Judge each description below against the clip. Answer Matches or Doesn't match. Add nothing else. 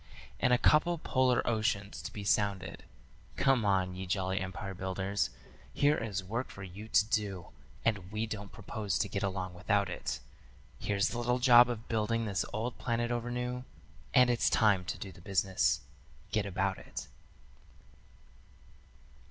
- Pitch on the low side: Matches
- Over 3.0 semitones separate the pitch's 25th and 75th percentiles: Matches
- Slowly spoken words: Doesn't match